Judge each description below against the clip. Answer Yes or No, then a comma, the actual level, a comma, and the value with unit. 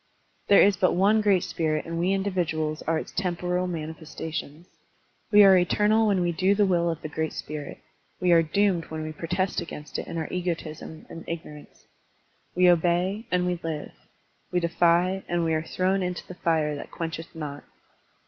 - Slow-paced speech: No, average, 185 wpm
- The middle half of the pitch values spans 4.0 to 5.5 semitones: No, narrow, 2.4 semitones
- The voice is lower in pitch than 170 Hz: No, medium, 175 Hz